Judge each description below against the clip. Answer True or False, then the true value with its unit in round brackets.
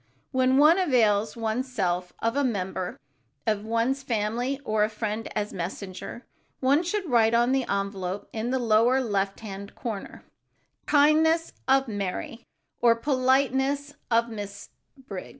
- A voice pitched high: True (230 Hz)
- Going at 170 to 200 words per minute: False (140 wpm)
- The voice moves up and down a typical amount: True (4.3 semitones)